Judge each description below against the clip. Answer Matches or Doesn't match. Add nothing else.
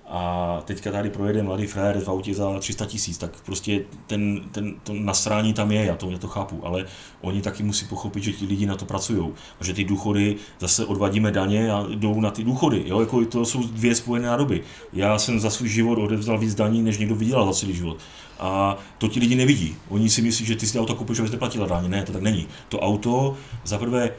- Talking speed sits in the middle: Doesn't match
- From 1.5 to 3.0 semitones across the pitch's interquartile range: Matches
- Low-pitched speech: Matches